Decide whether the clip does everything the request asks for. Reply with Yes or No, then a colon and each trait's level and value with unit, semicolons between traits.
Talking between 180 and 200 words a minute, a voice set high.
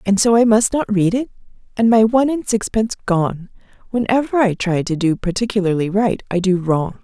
Yes: average, 195 wpm; high, 205 Hz